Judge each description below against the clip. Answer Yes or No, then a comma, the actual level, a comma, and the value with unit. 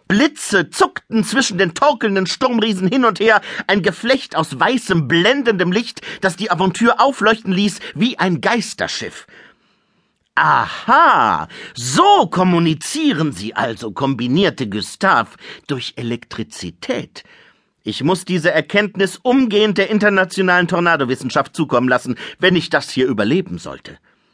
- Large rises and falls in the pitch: Yes, wide, 6.0 semitones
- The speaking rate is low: Yes, slow, 120 wpm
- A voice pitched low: No, high, 190 Hz